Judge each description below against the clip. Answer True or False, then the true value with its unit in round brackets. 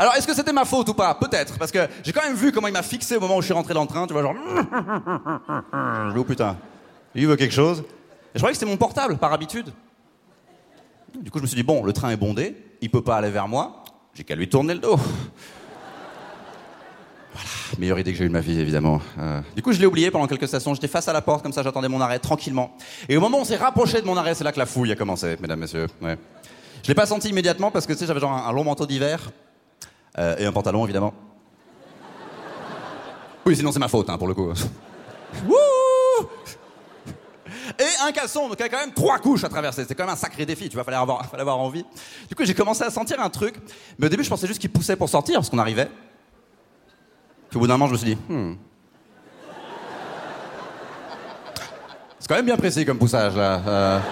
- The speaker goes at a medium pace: False (235 wpm)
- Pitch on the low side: False (145 Hz)